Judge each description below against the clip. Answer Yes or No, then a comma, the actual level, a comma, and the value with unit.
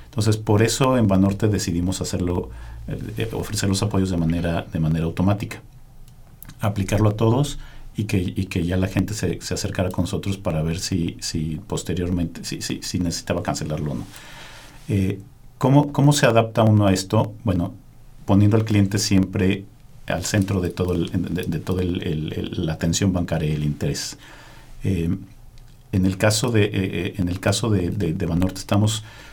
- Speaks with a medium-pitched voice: No, low, 100 Hz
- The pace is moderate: Yes, average, 170 wpm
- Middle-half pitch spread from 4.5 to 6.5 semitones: No, average, 3.7 semitones